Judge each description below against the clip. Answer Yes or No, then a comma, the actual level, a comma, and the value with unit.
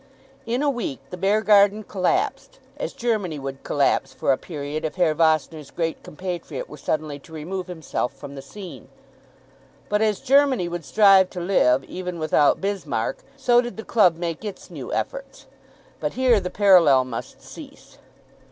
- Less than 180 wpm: Yes, average, 160 wpm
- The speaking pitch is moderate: Yes, medium, 180 Hz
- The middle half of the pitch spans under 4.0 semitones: No, average, 5.3 semitones